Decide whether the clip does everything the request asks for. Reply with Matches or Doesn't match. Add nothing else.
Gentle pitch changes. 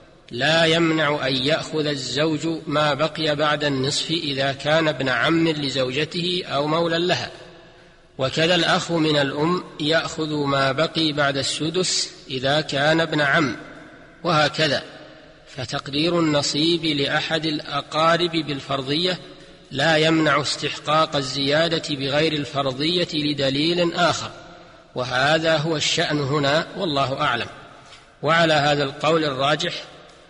Matches